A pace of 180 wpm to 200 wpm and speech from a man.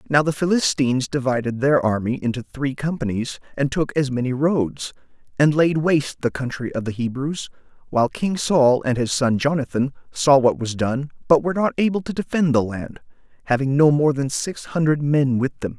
Yes: average, 190 wpm; male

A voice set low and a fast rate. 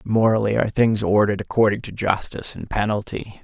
No: low, 105 Hz; average, 155 wpm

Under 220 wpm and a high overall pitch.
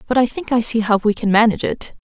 No: fast, 295 wpm; high, 225 Hz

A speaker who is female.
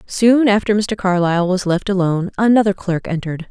Yes: female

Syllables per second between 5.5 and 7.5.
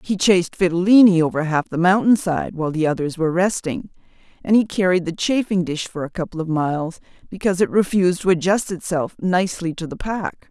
Yes: 6.0 syllables/s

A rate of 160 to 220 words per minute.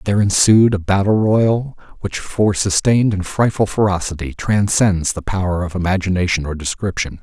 No: average, 150 wpm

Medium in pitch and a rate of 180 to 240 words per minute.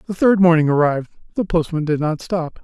Yes: medium, 165 Hz; fast, 205 wpm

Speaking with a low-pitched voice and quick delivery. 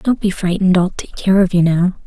No: medium, 185 Hz; fast, 230 wpm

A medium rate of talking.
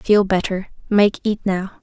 Yes: average, 165 wpm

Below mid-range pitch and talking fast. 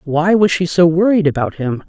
No: medium, 170 Hz; fast, 225 wpm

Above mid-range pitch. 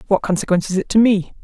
Yes: high, 195 Hz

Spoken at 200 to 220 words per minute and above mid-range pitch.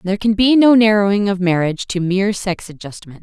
Yes: fast, 205 wpm; high, 195 Hz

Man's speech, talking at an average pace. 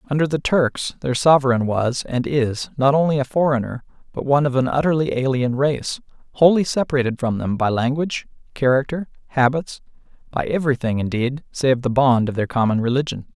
Yes: male; average, 165 wpm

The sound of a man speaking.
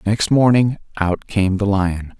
Yes: male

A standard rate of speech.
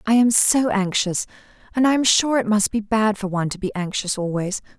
No: fast, 225 wpm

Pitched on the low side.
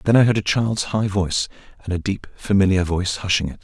Yes: very low, 95 Hz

